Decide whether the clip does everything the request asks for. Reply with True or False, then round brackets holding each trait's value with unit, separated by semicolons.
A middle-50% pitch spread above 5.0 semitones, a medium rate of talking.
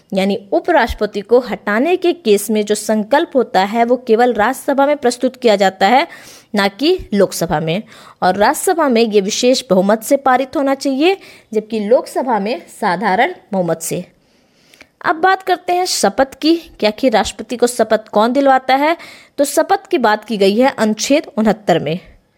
True (5.6 semitones; 170 wpm)